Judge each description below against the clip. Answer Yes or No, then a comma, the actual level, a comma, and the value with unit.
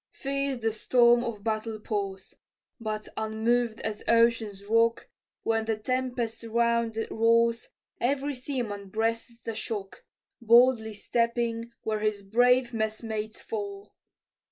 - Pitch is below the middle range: No, high, 230 Hz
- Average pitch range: No, narrow, 1.7 semitones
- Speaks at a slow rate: Yes, slow, 120 wpm